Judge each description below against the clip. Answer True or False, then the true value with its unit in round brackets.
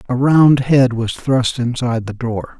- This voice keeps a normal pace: True (185 wpm)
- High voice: False (125 Hz)